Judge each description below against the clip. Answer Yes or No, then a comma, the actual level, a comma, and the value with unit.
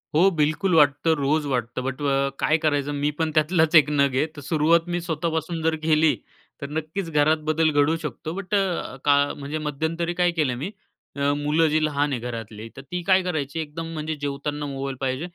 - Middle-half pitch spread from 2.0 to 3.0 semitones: Yes, narrow, 2.4 semitones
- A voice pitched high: No, medium, 150 Hz